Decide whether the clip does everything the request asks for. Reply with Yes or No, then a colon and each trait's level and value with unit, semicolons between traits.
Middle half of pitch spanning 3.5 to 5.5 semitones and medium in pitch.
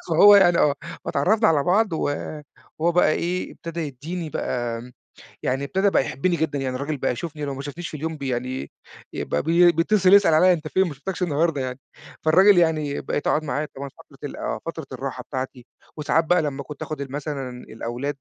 Yes: average, 3.9 semitones; medium, 155 Hz